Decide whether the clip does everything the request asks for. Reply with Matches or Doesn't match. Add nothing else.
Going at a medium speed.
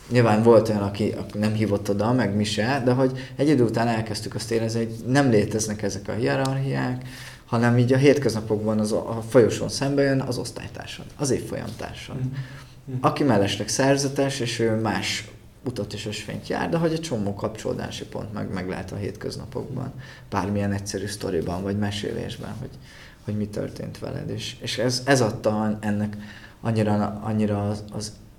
Doesn't match